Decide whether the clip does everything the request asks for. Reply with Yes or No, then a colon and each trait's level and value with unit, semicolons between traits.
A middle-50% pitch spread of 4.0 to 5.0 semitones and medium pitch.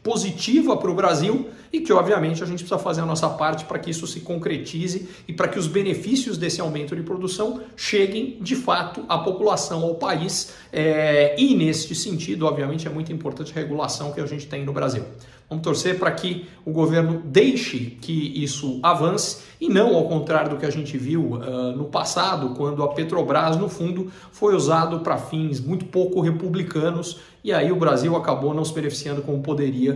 No: average, 3.6 semitones; medium, 165 Hz